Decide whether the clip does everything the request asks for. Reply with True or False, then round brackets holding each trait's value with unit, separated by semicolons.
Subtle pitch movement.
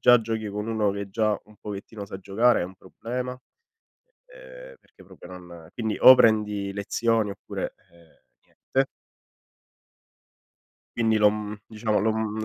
True (2.2 semitones)